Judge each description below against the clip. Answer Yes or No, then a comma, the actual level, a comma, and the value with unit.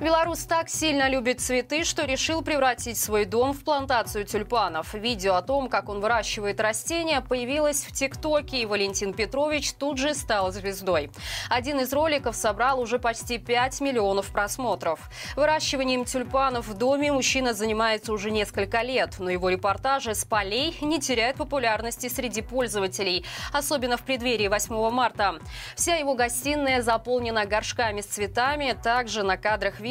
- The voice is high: Yes, high, 245 Hz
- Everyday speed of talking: Yes, average, 150 wpm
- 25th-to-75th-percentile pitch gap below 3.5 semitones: No, average, 4.5 semitones